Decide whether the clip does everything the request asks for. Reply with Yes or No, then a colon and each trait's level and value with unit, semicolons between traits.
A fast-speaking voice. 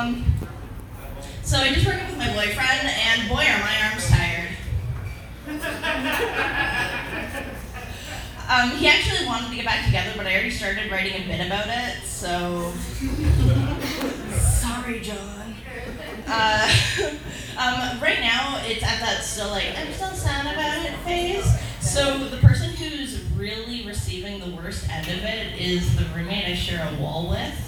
No: average, 150 wpm